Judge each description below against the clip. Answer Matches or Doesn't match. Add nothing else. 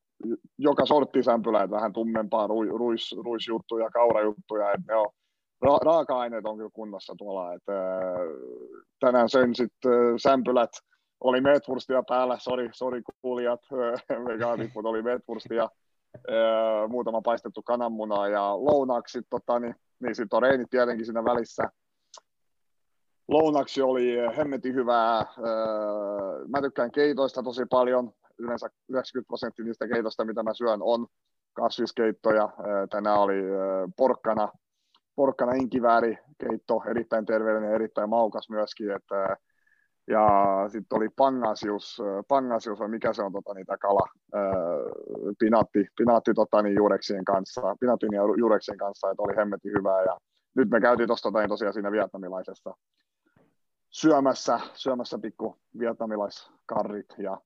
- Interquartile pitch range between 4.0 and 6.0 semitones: Doesn't match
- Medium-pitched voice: Doesn't match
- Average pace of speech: Matches